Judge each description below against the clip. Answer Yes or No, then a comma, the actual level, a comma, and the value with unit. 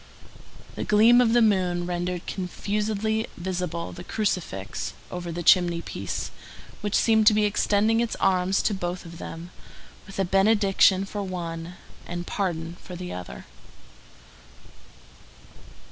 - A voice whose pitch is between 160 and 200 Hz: Yes, medium, 185 Hz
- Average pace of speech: No, slow, 130 wpm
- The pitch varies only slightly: No, average, 3.1 semitones